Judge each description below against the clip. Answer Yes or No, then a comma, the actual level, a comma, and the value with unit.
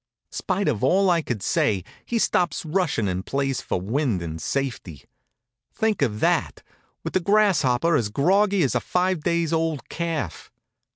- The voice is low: No, medium, 150 Hz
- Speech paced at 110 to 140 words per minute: No, average, 160 wpm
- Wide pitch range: Yes, wide, 7.6 semitones